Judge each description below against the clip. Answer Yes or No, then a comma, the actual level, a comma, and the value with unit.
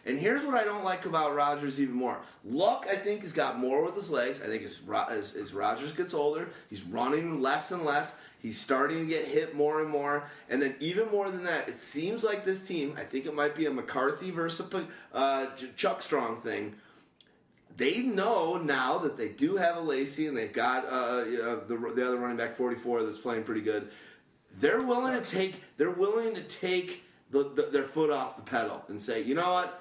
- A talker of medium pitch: Yes, medium, 155 Hz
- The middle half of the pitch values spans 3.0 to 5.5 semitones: Yes, average, 5.2 semitones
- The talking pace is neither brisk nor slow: No, fast, 210 wpm